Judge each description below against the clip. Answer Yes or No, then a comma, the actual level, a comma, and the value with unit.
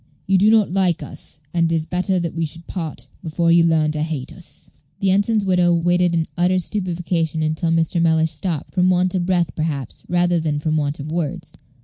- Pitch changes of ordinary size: No, narrow, 2.2 semitones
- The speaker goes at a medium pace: No, fast, 210 wpm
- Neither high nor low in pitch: Yes, medium, 170 Hz